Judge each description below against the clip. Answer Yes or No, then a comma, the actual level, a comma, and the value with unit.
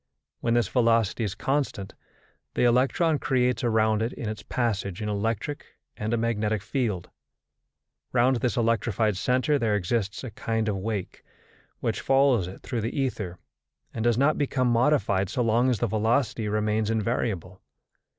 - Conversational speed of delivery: Yes, average, 155 wpm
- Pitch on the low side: Yes, low, 115 Hz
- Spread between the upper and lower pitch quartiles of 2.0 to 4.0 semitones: Yes, average, 2.9 semitones